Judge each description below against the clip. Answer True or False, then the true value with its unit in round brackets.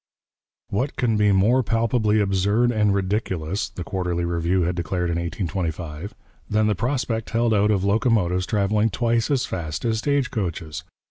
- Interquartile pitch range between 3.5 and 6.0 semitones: True (4.3 semitones)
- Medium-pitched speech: False (100 Hz)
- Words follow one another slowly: False (155 wpm)